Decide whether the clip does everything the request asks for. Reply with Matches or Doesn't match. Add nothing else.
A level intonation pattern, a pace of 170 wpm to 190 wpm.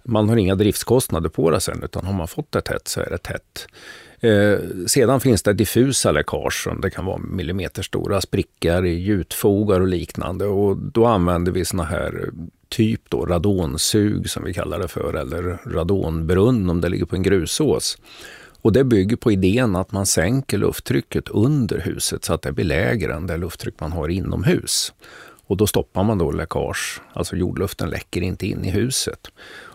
Doesn't match